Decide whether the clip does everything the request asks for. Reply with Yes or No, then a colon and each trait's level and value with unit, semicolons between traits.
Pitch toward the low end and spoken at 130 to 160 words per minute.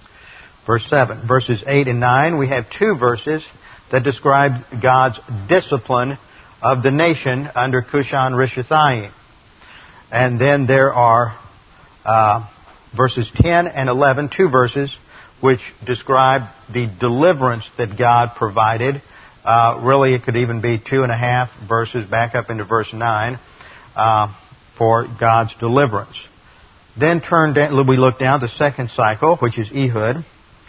Yes: low, 125 Hz; slow, 135 wpm